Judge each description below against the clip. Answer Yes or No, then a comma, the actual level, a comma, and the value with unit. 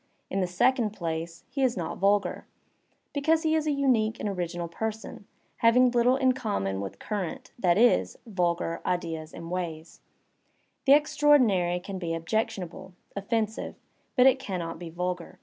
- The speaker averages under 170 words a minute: Yes, average, 160 wpm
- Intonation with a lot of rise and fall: Yes, wide, 6.3 semitones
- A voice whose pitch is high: Yes, high, 195 Hz